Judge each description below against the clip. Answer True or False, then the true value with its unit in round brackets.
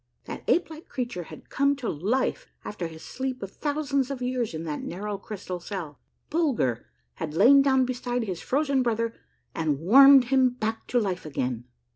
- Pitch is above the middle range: True (240 Hz)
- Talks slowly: False (175 wpm)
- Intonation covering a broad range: True (6.9 semitones)